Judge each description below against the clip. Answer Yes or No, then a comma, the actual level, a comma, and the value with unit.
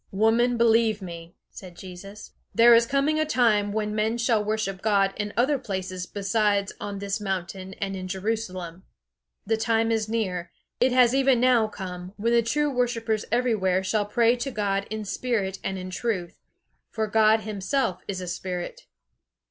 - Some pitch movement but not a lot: Yes, average, 3.4 semitones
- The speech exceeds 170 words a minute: No, average, 165 wpm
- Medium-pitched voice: No, high, 215 Hz